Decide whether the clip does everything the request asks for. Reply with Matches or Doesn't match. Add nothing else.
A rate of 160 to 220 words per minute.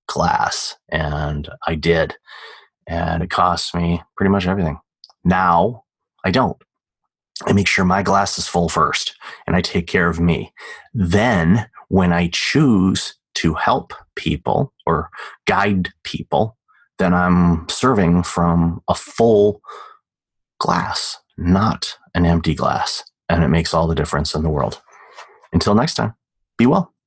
Doesn't match